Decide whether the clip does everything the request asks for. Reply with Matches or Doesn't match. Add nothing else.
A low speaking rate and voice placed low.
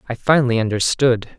Matches